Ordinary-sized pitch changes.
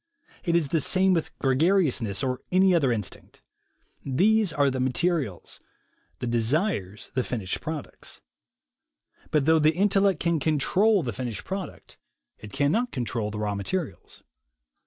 No: wide, 7.0 semitones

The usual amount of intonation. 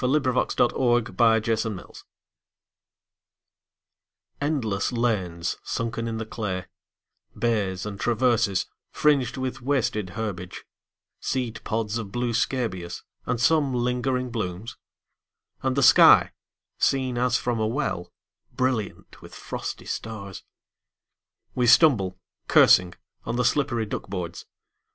Yes: average, 3.6 semitones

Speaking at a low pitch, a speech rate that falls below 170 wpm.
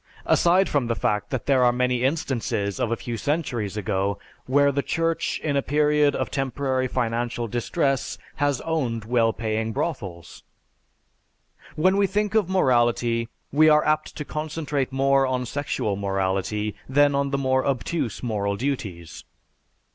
Yes: low, 130 Hz; average, 150 wpm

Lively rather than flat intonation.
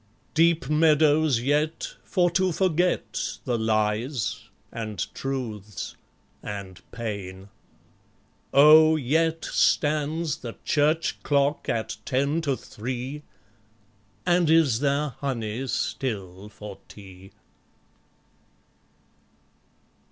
Yes: wide, 6.2 semitones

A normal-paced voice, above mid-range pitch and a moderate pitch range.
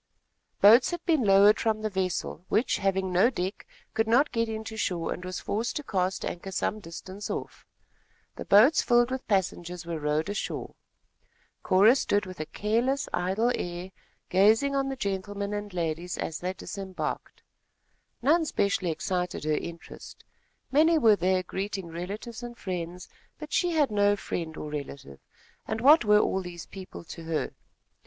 Yes: average, 160 wpm; high, 200 Hz; average, 4.1 semitones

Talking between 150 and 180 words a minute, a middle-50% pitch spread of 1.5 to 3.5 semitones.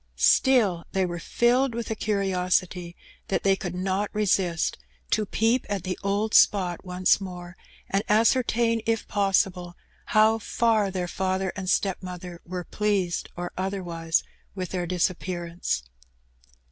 No: slow, 135 wpm; average, 2.8 semitones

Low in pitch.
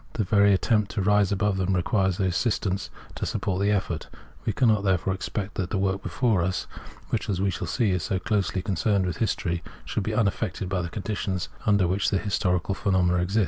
Yes: very low, 95 Hz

